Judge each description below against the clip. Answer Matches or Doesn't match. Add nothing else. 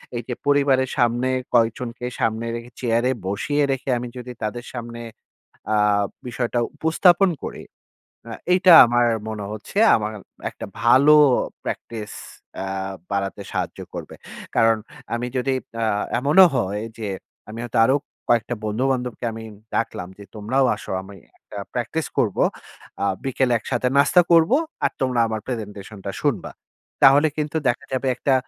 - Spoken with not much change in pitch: Doesn't match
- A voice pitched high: Doesn't match